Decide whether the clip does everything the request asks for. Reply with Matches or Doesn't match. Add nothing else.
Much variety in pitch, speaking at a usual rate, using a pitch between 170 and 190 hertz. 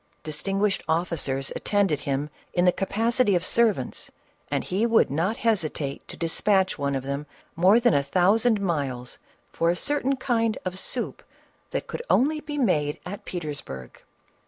Matches